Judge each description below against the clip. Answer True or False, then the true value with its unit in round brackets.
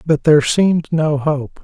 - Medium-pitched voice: True (155 Hz)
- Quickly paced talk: False (185 wpm)